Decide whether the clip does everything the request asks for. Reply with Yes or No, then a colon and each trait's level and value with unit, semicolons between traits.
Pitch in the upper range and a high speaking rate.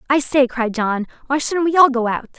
Yes: very high, 260 Hz; fast, 250 wpm